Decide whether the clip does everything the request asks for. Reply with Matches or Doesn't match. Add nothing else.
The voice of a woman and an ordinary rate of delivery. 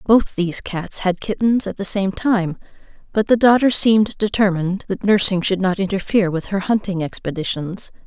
Matches